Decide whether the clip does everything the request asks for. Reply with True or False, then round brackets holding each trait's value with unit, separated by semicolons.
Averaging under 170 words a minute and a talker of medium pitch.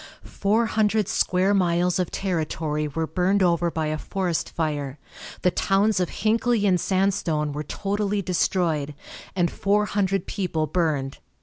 True (140 wpm; 180 Hz)